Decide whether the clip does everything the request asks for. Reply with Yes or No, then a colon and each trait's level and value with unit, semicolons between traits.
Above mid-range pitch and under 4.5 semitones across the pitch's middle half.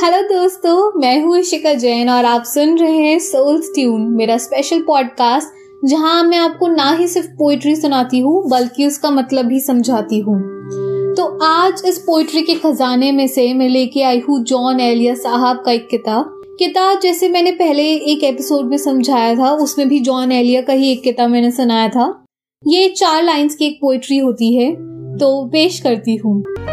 No: very high, 275 Hz; average, 5.0 semitones